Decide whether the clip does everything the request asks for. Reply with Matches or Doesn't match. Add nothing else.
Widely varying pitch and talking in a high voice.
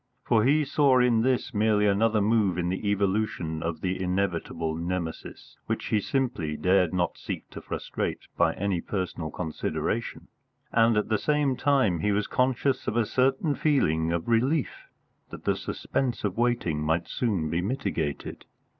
Doesn't match